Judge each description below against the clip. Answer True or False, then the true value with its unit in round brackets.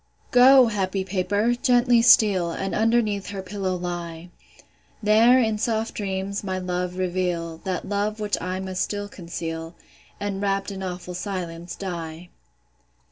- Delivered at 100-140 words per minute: True (135 wpm)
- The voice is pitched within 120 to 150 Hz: False (190 Hz)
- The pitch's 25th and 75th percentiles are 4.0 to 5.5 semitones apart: False (2.8 semitones)